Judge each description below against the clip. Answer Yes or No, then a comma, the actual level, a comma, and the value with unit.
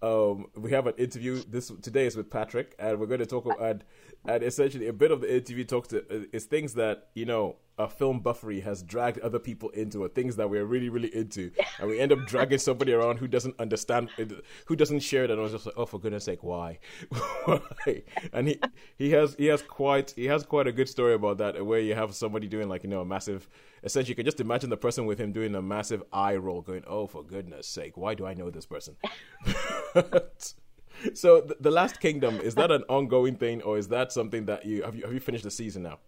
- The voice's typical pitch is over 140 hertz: No, low, 115 Hz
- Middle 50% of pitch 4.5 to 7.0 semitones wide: No, average, 3.6 semitones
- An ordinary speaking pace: No, fast, 240 wpm